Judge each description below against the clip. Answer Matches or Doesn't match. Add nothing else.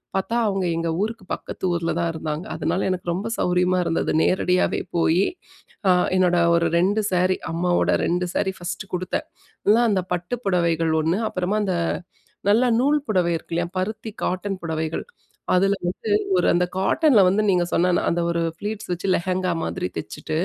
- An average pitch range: Doesn't match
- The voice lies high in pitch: Doesn't match